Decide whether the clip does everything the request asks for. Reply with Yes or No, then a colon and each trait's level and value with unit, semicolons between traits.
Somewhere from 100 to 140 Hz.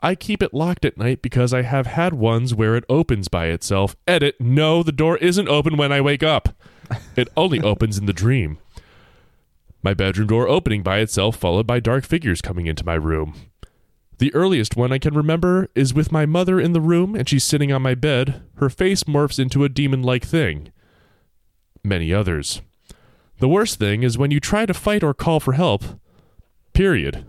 Yes: low, 135 Hz